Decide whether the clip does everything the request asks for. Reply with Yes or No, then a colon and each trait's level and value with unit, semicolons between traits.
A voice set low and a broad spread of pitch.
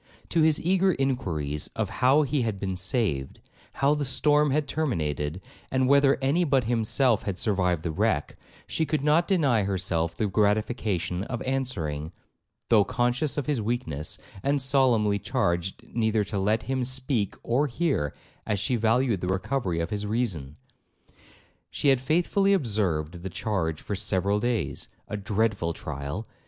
Yes: low, 110 Hz; wide, 6.4 semitones